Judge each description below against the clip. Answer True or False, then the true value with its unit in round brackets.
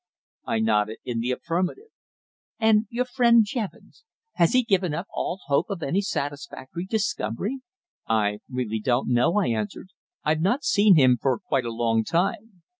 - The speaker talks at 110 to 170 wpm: True (160 wpm)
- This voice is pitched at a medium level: True (170 Hz)